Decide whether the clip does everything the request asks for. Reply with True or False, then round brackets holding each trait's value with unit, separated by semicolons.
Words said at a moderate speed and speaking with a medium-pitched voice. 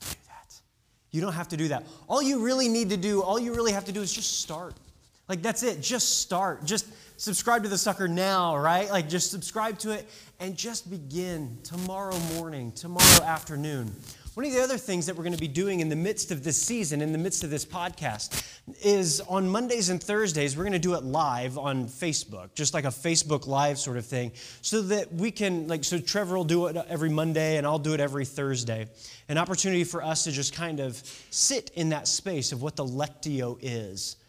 False (215 wpm; 165 Hz)